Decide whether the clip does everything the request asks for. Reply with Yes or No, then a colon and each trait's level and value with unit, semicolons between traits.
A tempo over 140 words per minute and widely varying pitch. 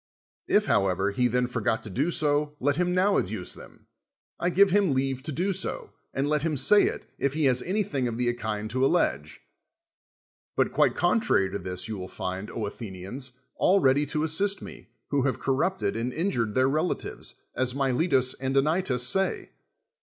Yes: average, 185 wpm; wide, 5.9 semitones